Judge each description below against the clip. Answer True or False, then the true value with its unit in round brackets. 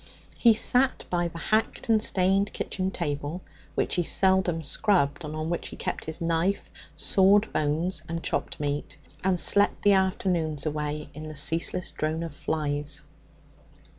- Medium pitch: True (165 Hz)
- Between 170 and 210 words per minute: False (155 wpm)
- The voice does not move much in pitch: False (3.8 semitones)